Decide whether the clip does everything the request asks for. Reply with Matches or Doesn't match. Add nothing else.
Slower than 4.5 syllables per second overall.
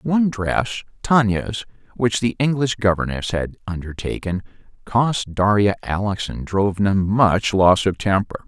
Matches